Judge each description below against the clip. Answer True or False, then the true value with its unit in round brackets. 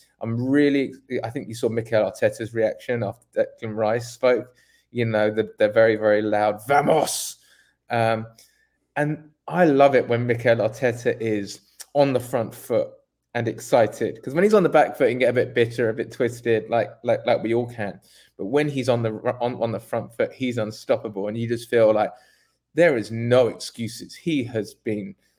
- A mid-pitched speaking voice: False (115 Hz)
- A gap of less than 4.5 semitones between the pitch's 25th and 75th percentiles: True (3.3 semitones)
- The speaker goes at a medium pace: True (195 wpm)